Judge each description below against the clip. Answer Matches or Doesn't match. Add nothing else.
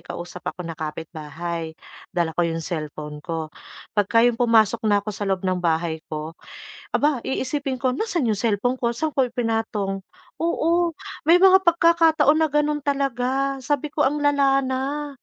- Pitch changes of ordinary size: Doesn't match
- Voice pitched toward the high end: Matches